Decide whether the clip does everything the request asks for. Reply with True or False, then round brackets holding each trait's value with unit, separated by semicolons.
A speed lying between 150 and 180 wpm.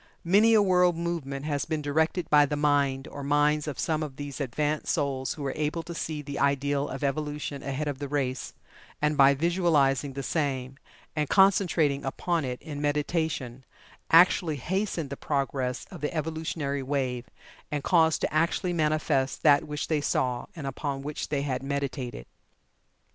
True (170 wpm)